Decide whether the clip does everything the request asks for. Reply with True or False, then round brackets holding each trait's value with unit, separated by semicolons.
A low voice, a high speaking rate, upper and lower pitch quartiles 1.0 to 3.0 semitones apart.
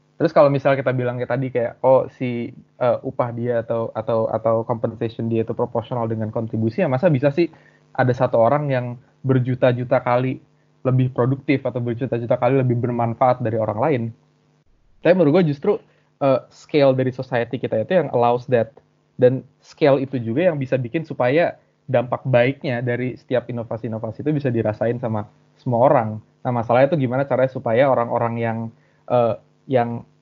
True (125 Hz; 165 wpm; 2.5 semitones)